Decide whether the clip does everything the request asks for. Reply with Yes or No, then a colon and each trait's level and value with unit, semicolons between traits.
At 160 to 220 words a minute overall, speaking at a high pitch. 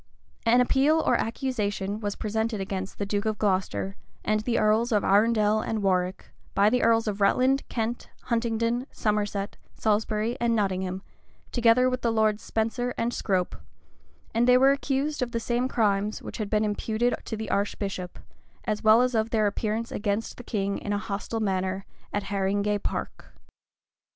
Yes: average, 170 wpm; high, 215 Hz